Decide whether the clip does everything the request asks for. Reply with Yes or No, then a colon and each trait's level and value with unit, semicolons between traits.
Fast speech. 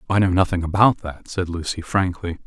No: average, 195 wpm